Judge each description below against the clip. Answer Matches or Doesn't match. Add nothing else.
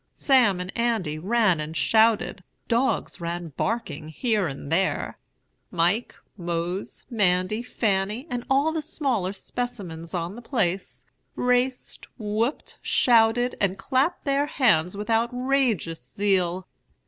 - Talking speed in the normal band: Doesn't match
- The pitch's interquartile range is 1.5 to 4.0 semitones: Doesn't match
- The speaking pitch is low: Doesn't match